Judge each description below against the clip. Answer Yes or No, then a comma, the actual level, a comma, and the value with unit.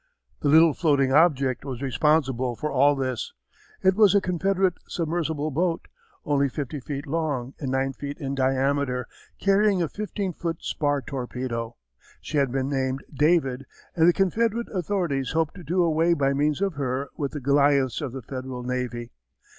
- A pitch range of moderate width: Yes, average, 4.0 semitones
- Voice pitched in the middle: Yes, medium, 145 Hz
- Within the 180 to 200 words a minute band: No, average, 165 wpm